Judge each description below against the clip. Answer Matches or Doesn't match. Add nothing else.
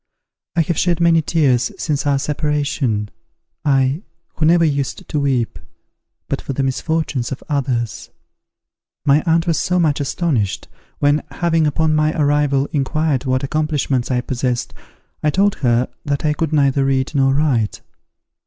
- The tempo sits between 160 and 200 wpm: Doesn't match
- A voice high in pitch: Doesn't match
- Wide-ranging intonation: Doesn't match